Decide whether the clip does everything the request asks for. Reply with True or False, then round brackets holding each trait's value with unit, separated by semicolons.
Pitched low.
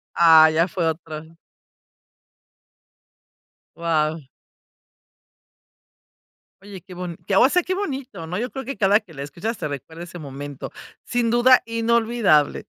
False (180 Hz)